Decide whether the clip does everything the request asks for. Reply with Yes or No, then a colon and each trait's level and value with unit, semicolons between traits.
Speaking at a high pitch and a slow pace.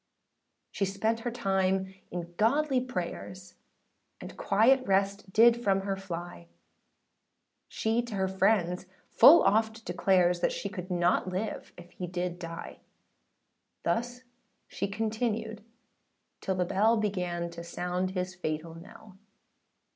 Yes: high, 195 Hz; slow, 125 wpm